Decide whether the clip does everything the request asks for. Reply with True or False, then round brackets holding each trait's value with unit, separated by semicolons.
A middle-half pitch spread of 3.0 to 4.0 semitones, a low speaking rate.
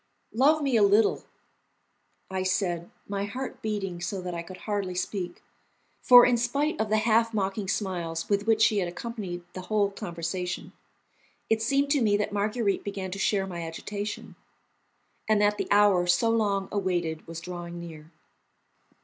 False (3.4 semitones; 165 wpm)